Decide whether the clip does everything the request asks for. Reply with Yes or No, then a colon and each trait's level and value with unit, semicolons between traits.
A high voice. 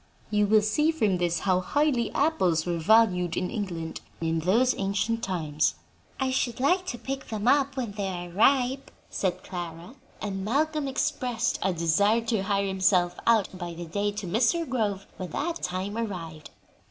Yes: high, 205 Hz